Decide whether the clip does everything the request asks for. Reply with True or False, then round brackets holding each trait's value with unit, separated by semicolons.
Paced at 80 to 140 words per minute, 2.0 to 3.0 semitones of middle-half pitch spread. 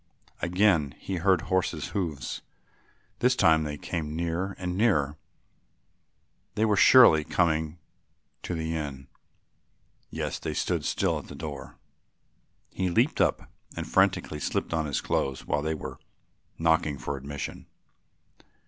False (135 wpm; 3.8 semitones)